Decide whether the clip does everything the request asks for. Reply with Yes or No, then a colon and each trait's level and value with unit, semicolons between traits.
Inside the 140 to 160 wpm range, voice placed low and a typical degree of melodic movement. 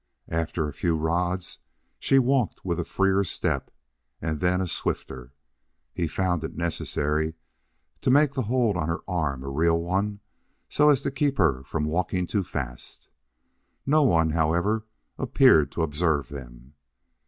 Yes: average, 155 wpm; very low, 85 Hz; average, 4.7 semitones